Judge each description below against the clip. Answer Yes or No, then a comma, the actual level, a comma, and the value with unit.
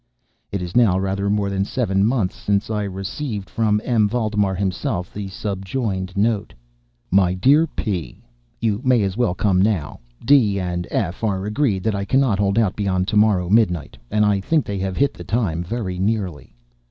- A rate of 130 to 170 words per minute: No, average, 180 wpm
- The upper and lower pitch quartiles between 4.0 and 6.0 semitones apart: No, average, 2.8 semitones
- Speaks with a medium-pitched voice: No, low, 100 Hz